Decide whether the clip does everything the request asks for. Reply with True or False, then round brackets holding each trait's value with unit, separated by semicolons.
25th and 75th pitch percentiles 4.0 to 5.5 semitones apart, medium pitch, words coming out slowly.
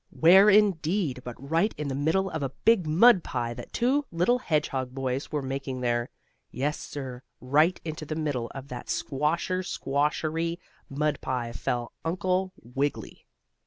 False (5.0 semitones; 150 Hz; 155 wpm)